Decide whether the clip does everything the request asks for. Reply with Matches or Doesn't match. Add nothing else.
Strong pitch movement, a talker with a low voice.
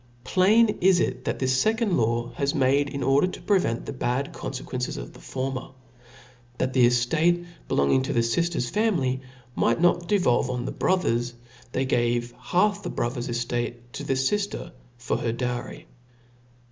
Matches